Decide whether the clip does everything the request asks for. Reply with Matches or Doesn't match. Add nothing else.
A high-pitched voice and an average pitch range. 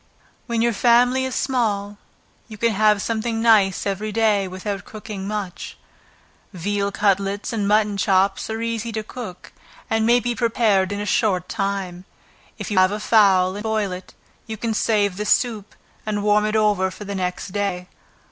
Doesn't match